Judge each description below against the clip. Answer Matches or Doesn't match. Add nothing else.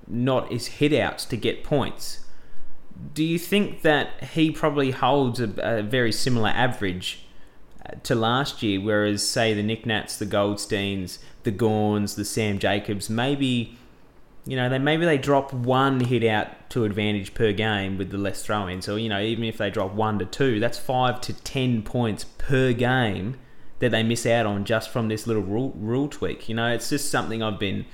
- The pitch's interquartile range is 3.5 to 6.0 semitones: Matches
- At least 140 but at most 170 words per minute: Doesn't match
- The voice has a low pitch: Matches